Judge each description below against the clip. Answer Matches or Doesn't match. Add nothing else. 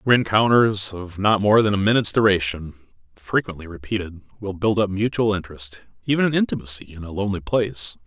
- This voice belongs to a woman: Doesn't match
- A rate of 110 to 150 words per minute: Doesn't match